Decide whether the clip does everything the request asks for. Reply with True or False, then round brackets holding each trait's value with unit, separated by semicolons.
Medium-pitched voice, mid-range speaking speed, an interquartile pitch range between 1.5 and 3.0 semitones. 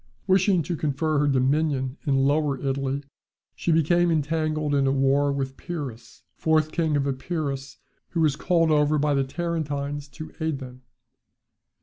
True (145 Hz; 150 wpm; 2.6 semitones)